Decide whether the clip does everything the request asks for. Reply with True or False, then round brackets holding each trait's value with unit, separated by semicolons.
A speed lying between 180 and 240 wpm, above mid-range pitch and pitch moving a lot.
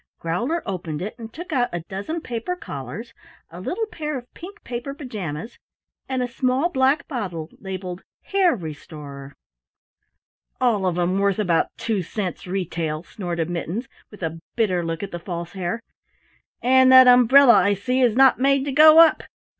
False (165 wpm; 215 Hz; 7.0 semitones)